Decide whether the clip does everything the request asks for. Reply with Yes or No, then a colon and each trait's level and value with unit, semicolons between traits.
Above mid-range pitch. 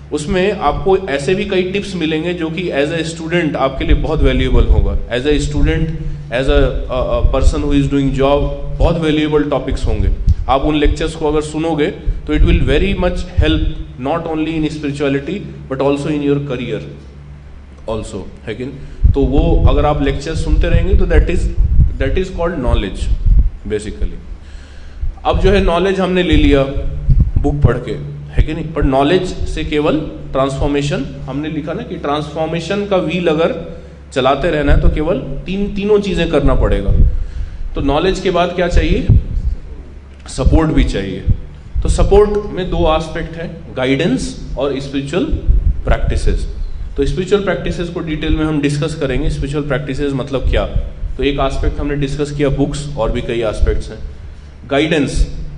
No: medium, 140 Hz